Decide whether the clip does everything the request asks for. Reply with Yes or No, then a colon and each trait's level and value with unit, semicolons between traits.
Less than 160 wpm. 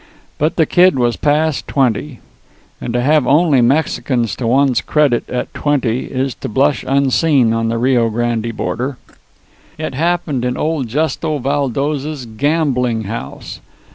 Yes: average, 140 wpm